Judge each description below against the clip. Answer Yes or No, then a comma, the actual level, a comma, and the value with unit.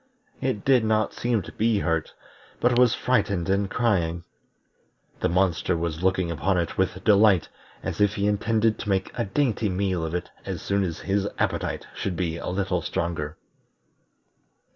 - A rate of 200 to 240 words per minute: No, average, 165 wpm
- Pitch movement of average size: Yes, average, 3.7 semitones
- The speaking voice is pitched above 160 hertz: No, very low, 95 Hz